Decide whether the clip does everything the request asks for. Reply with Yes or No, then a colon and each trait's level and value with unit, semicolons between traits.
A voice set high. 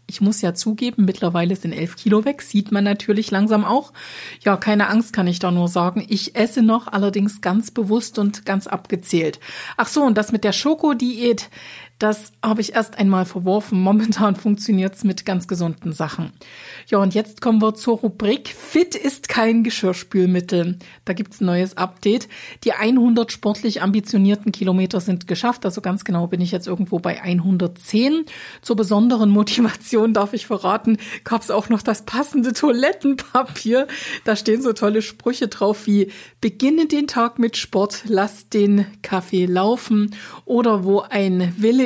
Yes: high, 210 Hz